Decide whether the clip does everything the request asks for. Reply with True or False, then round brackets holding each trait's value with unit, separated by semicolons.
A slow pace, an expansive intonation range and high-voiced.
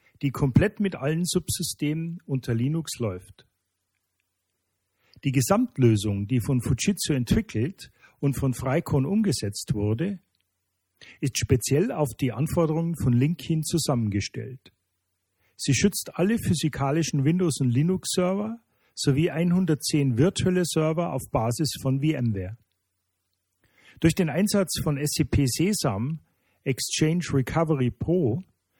False (105 wpm; 6.7 semitones; 140 Hz)